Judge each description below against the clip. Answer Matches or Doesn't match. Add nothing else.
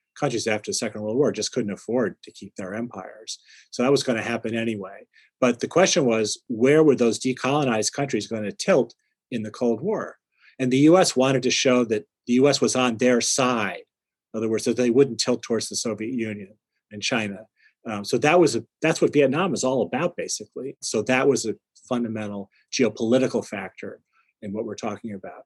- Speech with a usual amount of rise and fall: Matches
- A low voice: Matches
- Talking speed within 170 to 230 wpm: Matches